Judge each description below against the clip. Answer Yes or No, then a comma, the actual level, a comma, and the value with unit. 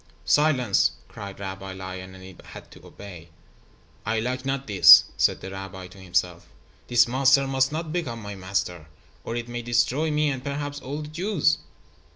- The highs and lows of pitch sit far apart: Yes, wide, 6.6 semitones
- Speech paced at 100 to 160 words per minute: No, average, 175 wpm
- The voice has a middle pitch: No, low, 120 Hz